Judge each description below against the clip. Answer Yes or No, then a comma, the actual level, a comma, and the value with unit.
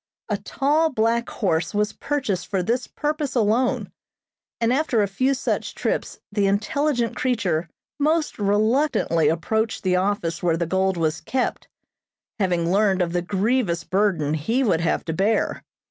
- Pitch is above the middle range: Yes, high, 205 Hz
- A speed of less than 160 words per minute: Yes, average, 150 wpm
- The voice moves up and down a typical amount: No, wide, 6.0 semitones